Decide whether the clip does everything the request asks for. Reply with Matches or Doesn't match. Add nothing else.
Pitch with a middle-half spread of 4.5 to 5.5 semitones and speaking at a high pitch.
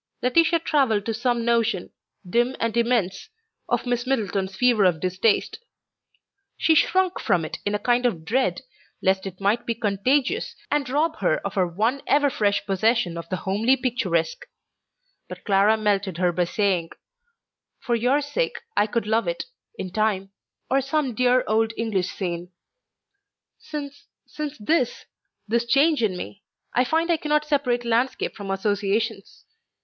Matches